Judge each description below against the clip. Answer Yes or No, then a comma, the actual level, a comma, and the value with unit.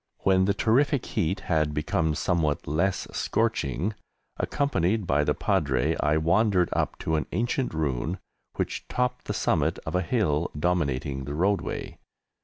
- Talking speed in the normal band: Yes, average, 145 wpm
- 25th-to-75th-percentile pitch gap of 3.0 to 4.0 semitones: No, average, 5.1 semitones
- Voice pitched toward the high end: No, very low, 85 Hz